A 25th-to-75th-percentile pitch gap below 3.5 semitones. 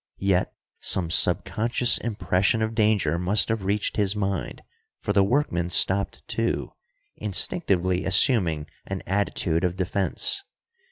Yes: average, 2.9 semitones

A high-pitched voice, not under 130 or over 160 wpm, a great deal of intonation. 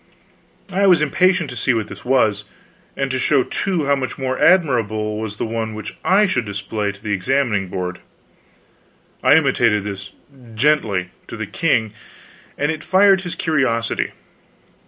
No: low, 125 Hz; average, 155 wpm; wide, 6.3 semitones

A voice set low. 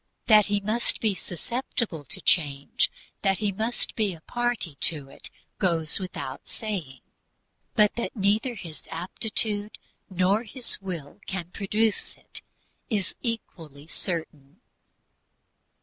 No: high, 195 Hz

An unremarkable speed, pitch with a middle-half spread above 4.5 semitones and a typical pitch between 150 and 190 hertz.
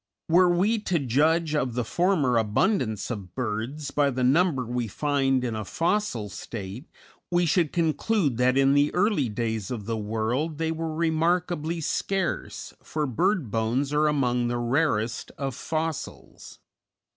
No: average, 150 wpm; wide, 5.6 semitones; medium, 140 Hz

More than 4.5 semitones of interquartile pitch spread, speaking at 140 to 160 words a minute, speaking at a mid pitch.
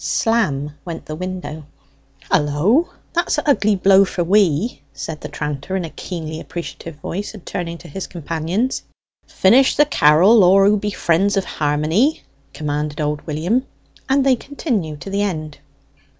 Yes: wide, 5.4 semitones; average, 155 wpm; medium, 180 Hz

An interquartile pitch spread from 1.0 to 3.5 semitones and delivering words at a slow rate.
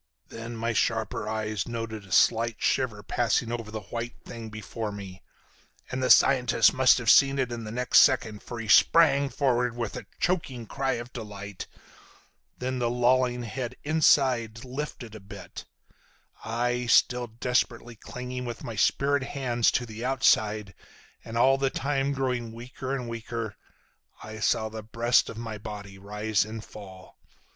No: narrow, 2.5 semitones; average, 155 wpm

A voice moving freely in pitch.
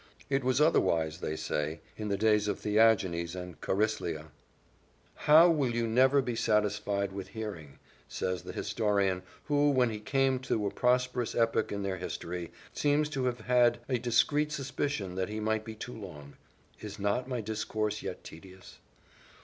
No: average, 4.8 semitones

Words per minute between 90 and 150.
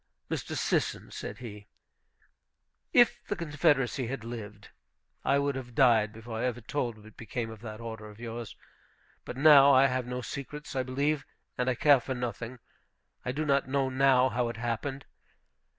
No: average, 170 wpm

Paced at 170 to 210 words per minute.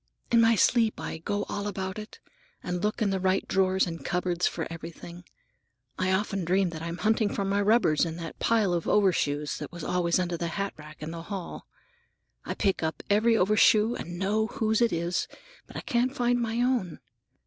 Yes: average, 195 wpm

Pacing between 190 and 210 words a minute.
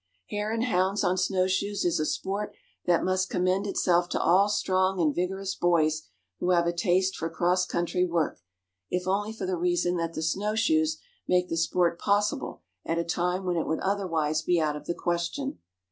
Yes: average, 195 wpm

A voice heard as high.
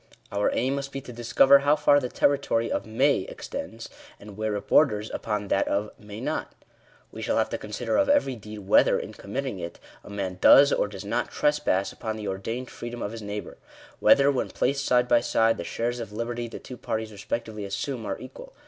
No: low, 115 Hz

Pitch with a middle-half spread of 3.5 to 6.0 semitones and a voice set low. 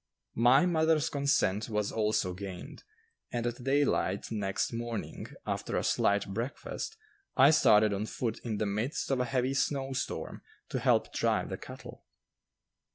Yes: average, 4.6 semitones; low, 120 Hz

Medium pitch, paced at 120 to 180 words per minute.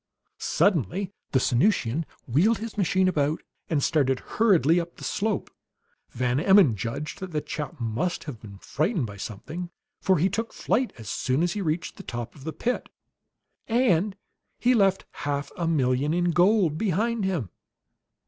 Yes: medium, 165 Hz; average, 160 wpm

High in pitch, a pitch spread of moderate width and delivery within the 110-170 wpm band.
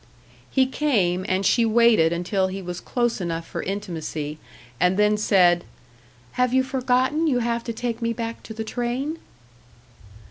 Yes: high, 220 Hz; average, 5.0 semitones; average, 155 wpm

